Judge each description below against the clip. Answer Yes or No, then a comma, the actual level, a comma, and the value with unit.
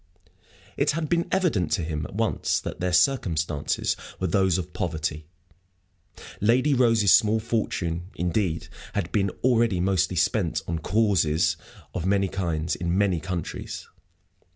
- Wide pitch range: No, average, 4.7 semitones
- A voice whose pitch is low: Yes, very low, 90 Hz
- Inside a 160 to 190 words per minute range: No, slow, 135 wpm